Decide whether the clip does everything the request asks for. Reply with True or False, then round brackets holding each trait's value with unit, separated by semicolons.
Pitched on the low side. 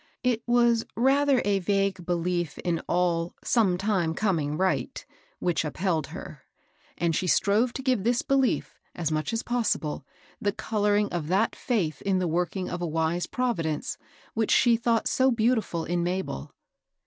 False (190 Hz)